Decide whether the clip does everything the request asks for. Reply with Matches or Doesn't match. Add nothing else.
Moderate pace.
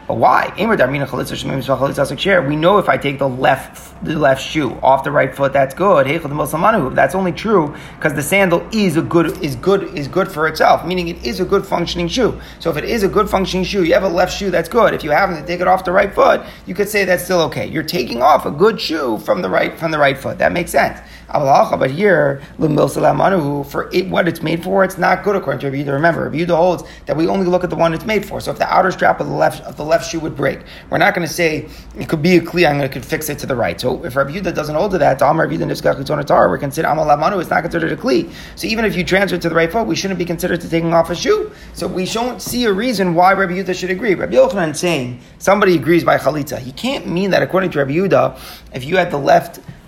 Doesn't match